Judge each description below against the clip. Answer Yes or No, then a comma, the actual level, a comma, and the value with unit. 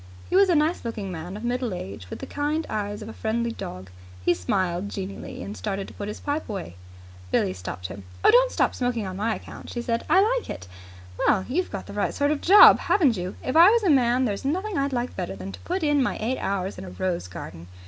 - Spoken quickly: Yes, fast, 245 wpm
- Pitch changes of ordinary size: No, wide, 7.7 semitones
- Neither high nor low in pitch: No, high, 225 Hz